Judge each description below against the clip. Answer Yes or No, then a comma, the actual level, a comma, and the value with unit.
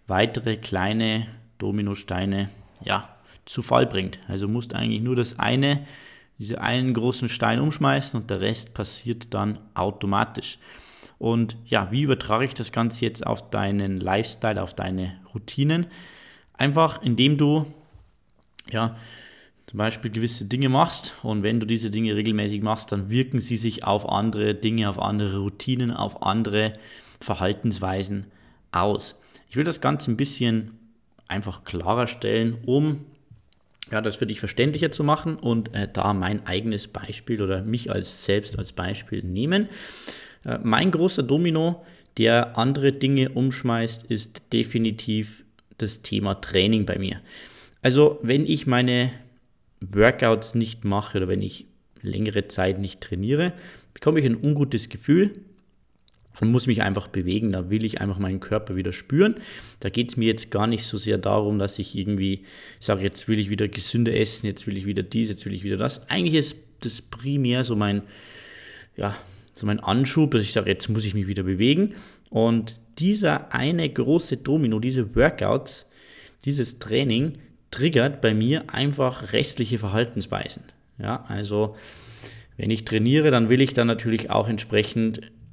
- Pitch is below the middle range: Yes, low, 115 Hz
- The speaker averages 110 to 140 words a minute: No, average, 155 wpm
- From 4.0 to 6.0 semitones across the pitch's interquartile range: No, average, 3.6 semitones